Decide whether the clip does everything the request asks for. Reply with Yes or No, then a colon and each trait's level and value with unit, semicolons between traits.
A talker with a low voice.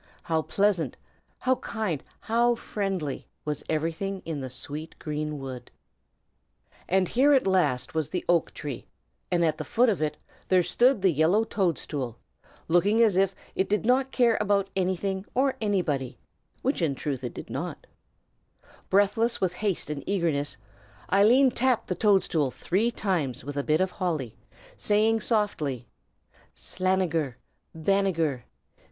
No: medium, 185 Hz